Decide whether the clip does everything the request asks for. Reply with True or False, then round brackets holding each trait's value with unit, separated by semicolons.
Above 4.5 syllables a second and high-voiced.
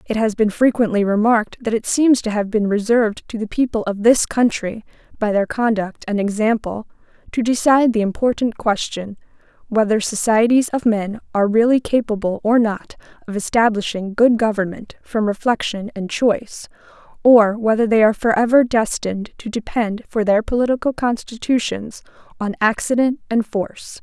True (5.2 syllables/s; 220 Hz)